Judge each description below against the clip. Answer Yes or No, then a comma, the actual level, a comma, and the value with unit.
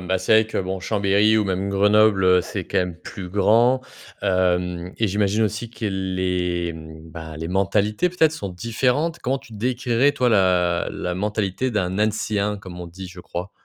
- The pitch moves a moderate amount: Yes, average, 3.3 semitones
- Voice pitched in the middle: No, low, 100 Hz